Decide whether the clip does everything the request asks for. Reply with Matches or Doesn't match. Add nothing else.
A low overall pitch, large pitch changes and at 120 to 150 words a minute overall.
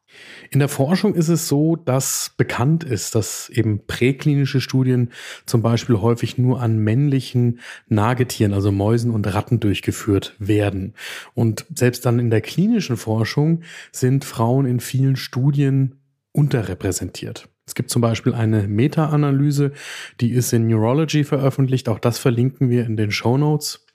Doesn't match